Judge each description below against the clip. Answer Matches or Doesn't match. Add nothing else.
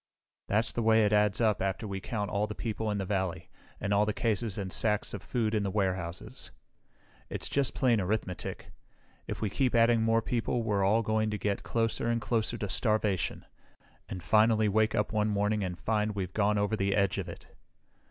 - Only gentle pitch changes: Matches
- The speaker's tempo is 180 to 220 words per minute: Matches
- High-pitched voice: Doesn't match